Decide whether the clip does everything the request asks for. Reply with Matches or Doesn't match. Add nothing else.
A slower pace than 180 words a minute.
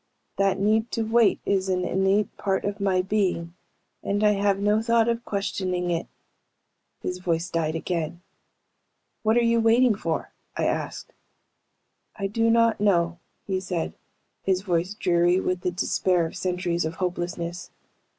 Matches